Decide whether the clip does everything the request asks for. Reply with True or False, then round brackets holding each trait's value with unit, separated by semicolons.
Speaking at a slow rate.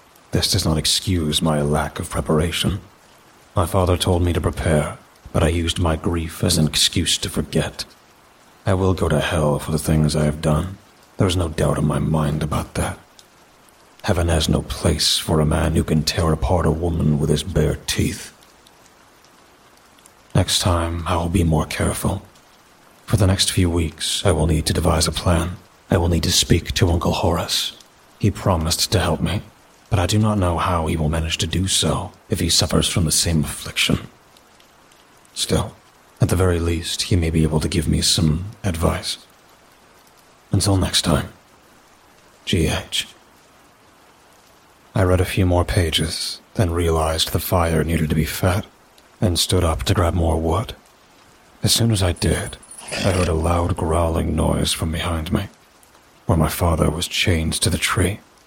False (180 wpm)